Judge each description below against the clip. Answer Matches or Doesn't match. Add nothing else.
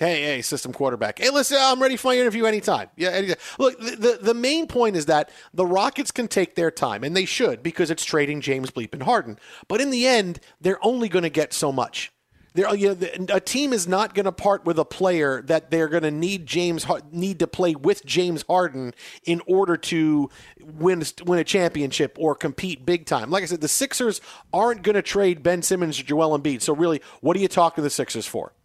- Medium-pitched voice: Matches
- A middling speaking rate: Doesn't match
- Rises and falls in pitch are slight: Doesn't match